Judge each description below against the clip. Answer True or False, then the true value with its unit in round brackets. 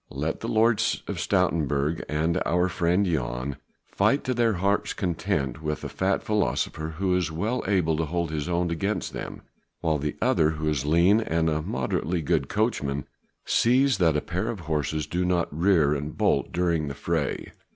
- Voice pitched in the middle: False (85 Hz)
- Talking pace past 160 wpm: True (180 wpm)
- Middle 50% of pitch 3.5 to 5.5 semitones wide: True (3.8 semitones)